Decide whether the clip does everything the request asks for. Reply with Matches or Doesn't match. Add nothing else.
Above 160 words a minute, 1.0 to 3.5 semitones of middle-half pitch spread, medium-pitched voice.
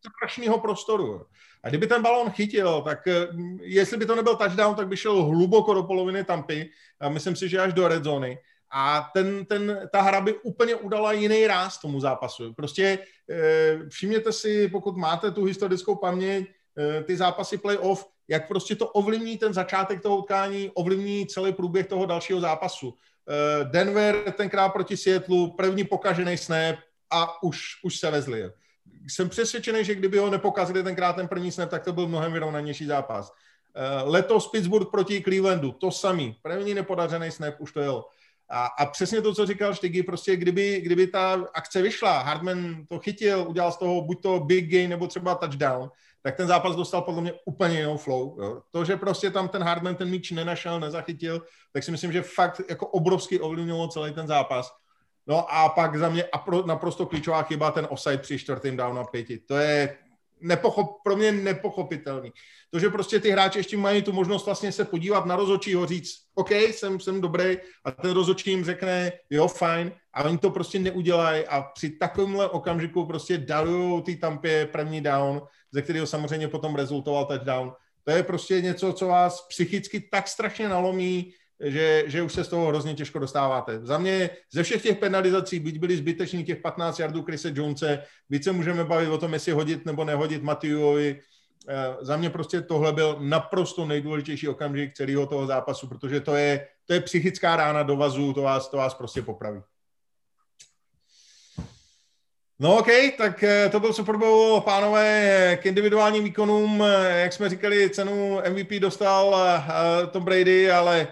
Doesn't match